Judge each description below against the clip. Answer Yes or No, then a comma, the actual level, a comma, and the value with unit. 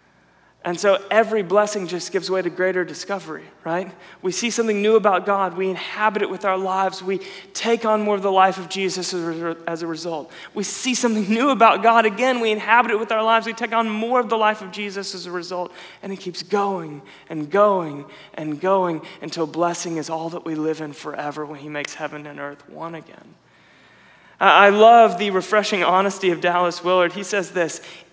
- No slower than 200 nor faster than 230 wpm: Yes, fast, 205 wpm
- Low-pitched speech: No, high, 190 Hz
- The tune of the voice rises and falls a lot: No, average, 3.6 semitones